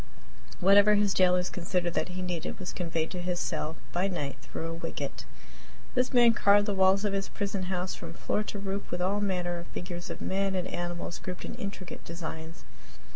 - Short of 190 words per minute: No, average, 195 wpm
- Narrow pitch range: Yes, narrow, 2.2 semitones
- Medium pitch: Yes, medium, 180 Hz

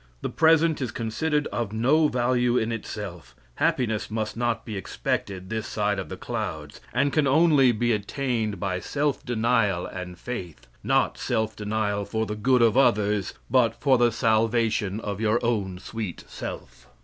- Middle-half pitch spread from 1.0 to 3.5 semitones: Yes, average, 3.2 semitones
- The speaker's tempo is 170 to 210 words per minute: No, average, 160 wpm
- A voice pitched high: No, low, 110 Hz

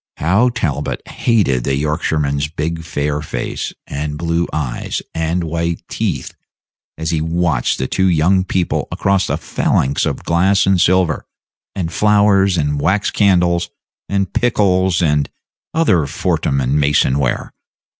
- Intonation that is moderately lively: Yes, average, 4.2 semitones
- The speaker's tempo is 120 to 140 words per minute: Yes, slow, 135 wpm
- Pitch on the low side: Yes, very low, 85 Hz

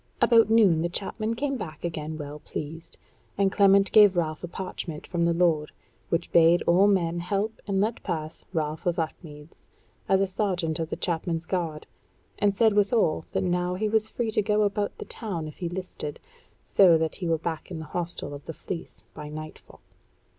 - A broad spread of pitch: No, average, 3.7 semitones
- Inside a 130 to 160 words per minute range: No, average, 190 wpm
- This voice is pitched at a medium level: Yes, medium, 175 Hz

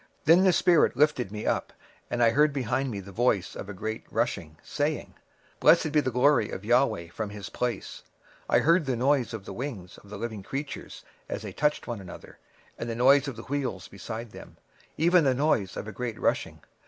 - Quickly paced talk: Yes, fast, 220 wpm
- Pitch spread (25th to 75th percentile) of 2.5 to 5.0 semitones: No, wide, 5.5 semitones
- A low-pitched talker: Yes, low, 120 Hz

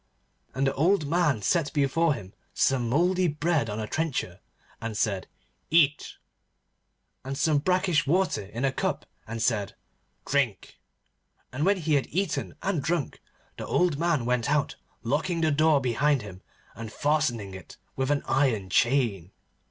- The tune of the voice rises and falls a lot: Yes, wide, 5.7 semitones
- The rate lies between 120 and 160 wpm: Yes, average, 150 wpm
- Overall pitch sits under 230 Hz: Yes, medium, 140 Hz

